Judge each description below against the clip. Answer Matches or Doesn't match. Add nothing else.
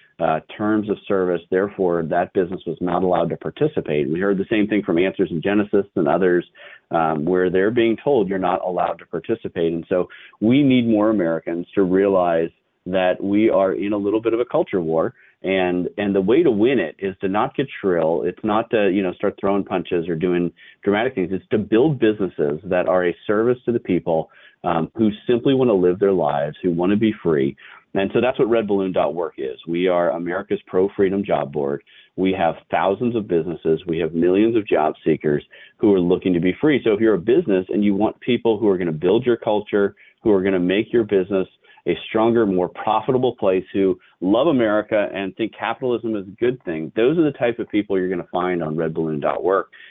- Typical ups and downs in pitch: Matches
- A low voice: Matches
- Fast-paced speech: Matches